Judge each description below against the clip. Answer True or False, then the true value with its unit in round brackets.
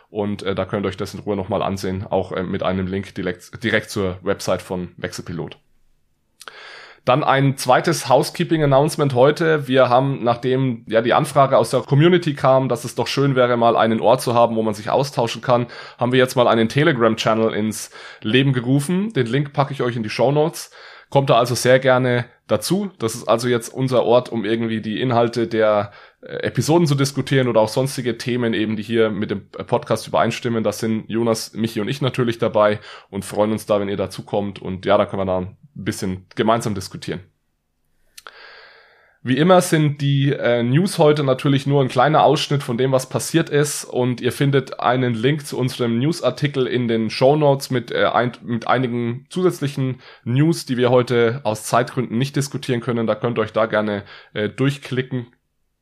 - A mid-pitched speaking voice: False (120 Hz)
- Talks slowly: False (190 wpm)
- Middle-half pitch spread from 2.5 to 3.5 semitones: False (3.9 semitones)